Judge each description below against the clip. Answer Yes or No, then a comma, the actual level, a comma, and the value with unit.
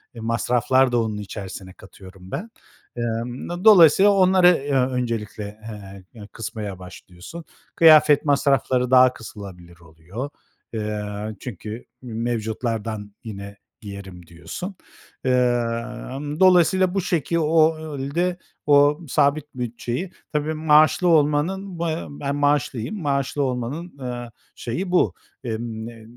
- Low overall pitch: Yes, low, 125 Hz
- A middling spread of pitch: No, wide, 5.8 semitones